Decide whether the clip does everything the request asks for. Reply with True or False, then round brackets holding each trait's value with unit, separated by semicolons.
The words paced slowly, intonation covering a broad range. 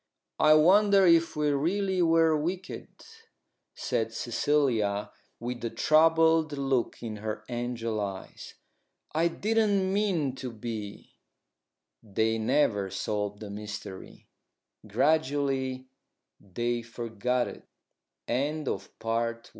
True (100 wpm; 6.4 semitones)